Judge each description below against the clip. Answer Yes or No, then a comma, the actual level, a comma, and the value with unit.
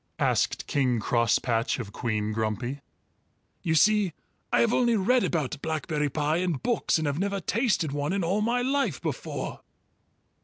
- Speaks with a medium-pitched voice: Yes, medium, 160 Hz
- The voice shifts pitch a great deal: Yes, wide, 8.4 semitones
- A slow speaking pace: No, average, 155 wpm